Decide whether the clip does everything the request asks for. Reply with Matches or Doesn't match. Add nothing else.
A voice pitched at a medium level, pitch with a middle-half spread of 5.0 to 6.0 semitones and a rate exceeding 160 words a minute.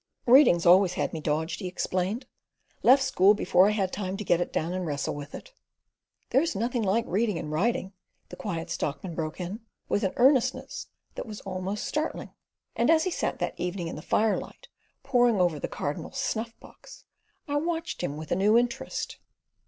Doesn't match